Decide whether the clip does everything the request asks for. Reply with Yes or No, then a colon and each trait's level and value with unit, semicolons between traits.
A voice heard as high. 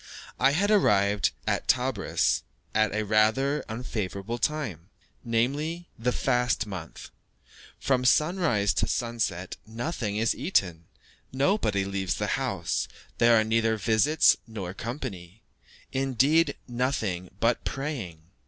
No: low, 115 Hz